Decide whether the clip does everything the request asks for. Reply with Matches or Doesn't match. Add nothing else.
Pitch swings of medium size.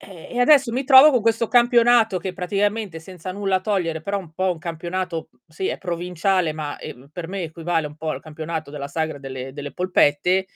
Matches